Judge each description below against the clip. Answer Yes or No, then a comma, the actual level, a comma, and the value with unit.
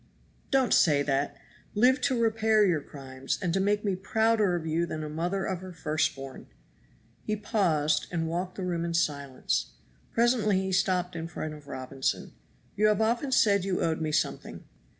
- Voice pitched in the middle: Yes, medium, 180 Hz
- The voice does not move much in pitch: No, average, 5.3 semitones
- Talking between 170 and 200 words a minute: Yes, average, 180 wpm